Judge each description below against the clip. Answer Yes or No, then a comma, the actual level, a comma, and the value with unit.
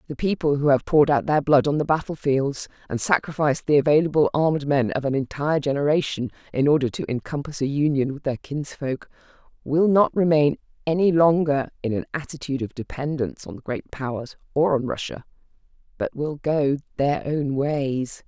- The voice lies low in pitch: No, medium, 145 Hz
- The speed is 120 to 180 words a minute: Yes, average, 175 wpm